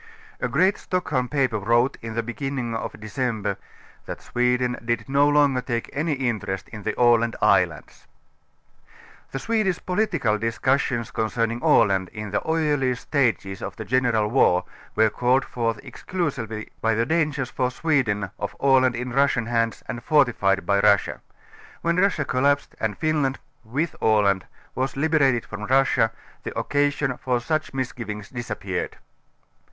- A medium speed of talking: Yes, average, 150 wpm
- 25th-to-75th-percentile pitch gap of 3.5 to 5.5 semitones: Yes, average, 4.0 semitones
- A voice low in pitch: Yes, low, 125 Hz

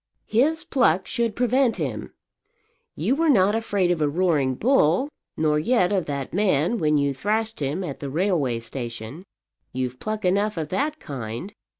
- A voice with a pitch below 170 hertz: No, medium, 180 Hz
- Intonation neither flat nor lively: No, wide, 7.3 semitones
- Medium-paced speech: Yes, average, 165 wpm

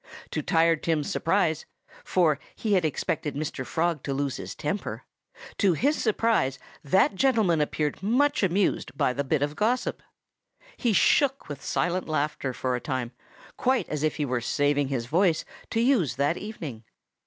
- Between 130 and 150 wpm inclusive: No, average, 165 wpm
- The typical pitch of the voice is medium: Yes, medium, 160 Hz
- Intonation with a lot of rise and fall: Yes, wide, 6.1 semitones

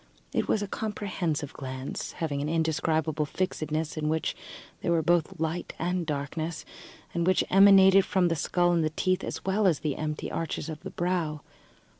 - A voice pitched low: No, medium, 165 Hz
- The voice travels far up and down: No, average, 3.0 semitones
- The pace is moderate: Yes, average, 170 wpm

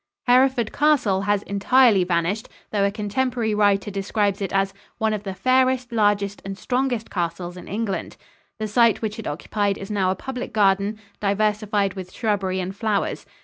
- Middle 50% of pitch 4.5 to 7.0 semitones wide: No, narrow, 2.6 semitones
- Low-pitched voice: No, high, 205 Hz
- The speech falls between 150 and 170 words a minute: Yes, average, 165 wpm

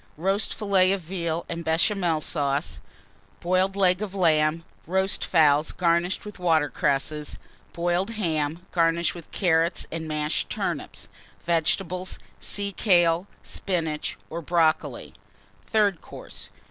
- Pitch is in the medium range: Yes, medium, 170 Hz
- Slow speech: Yes, slow, 120 wpm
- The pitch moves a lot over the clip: No, average, 2.8 semitones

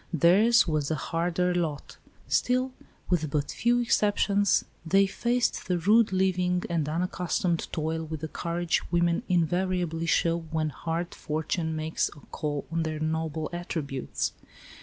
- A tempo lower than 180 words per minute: Yes, average, 140 wpm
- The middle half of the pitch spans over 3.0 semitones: No, narrow, 2.5 semitones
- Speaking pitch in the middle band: Yes, medium, 170 Hz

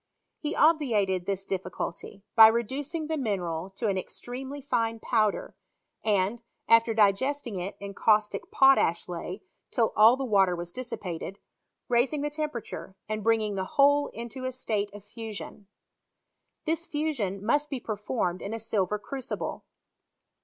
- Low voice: No, high, 225 Hz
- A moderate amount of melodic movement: Yes, average, 5.0 semitones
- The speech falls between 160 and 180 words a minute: No, average, 140 wpm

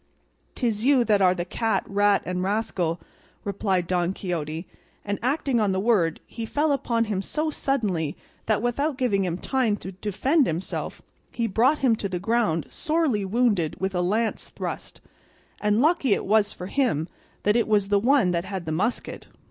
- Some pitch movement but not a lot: Yes, average, 4.6 semitones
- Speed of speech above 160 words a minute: Yes, average, 180 wpm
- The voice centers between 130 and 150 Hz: No, high, 210 Hz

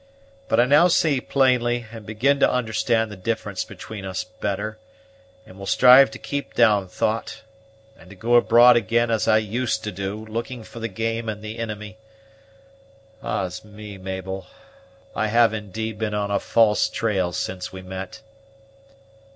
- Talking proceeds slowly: No, average, 160 wpm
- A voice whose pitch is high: No, low, 110 Hz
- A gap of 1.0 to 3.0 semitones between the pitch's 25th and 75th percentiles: Yes, average, 2.7 semitones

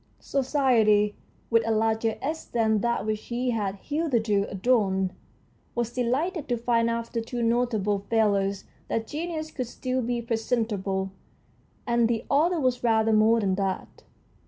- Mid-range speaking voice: No, high, 230 Hz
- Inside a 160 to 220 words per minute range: No, average, 140 wpm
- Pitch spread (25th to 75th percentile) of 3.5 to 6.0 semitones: No, narrow, 2.6 semitones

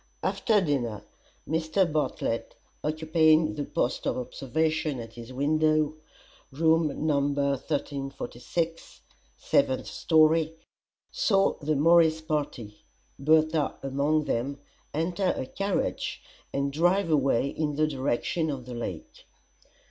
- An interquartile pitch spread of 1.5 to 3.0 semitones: Yes, average, 2.7 semitones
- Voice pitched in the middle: Yes, medium, 155 Hz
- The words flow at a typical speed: No, slow, 110 wpm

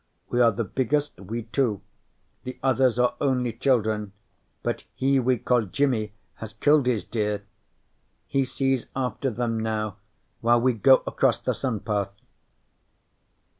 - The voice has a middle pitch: No, low, 120 Hz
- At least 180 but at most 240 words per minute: No, average, 140 wpm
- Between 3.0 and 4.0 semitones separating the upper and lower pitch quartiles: Yes, average, 3.3 semitones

